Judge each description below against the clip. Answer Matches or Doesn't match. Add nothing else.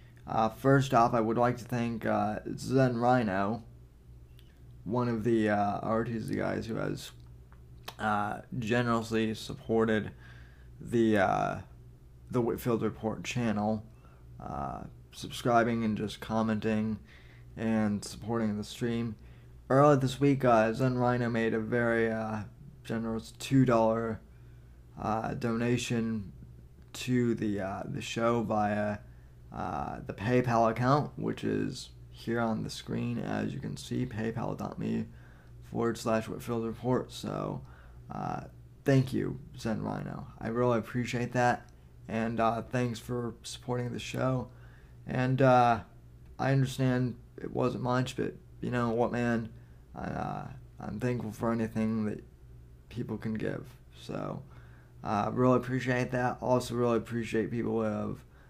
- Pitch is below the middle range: Matches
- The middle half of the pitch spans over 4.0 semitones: Matches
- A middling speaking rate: Doesn't match